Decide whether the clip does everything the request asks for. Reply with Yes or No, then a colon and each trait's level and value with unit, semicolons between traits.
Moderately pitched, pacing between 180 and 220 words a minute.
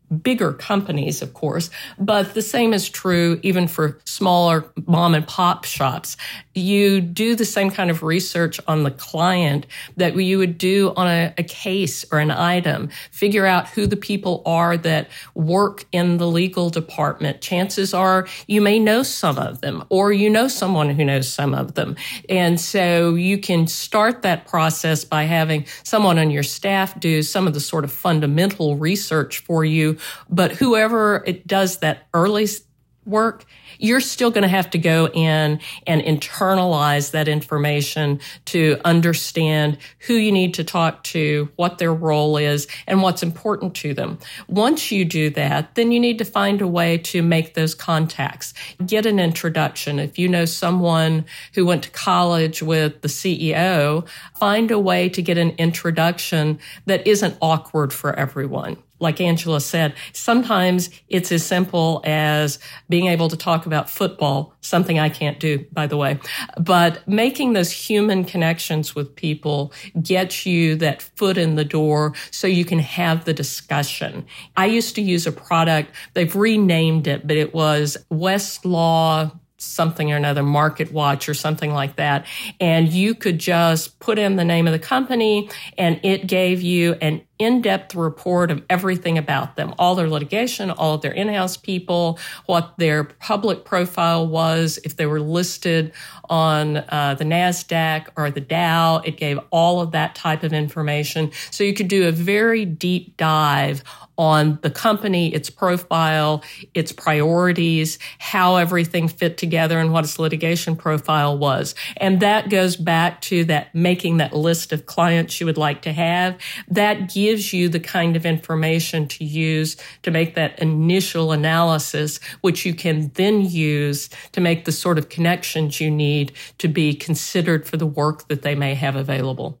No: medium, 165 Hz; average, 170 wpm